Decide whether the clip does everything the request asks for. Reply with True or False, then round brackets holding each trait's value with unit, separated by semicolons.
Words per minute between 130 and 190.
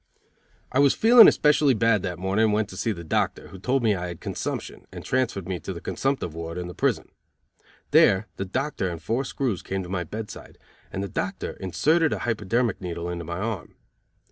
False (205 wpm)